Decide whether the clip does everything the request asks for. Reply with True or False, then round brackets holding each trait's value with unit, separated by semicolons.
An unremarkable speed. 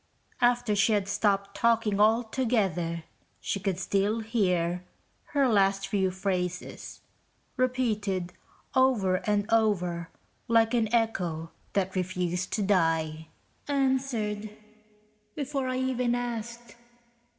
False (105 wpm)